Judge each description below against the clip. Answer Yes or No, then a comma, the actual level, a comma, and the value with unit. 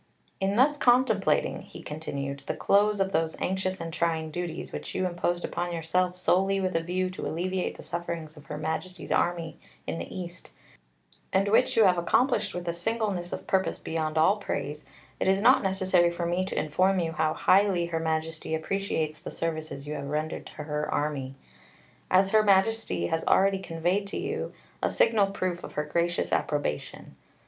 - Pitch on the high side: No, medium, 175 Hz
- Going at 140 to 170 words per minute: No, average, 180 wpm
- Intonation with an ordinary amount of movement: Yes, average, 3.2 semitones